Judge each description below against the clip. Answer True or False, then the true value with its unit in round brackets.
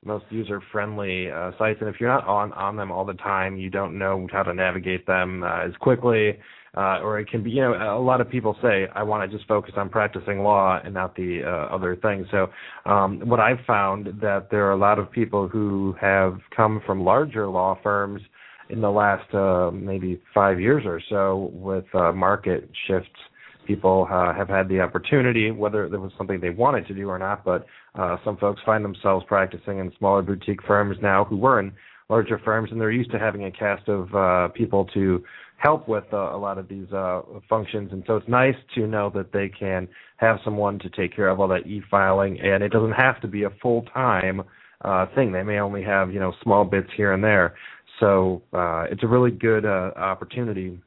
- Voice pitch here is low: True (100 Hz)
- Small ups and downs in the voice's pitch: True (2.1 semitones)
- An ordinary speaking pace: False (215 wpm)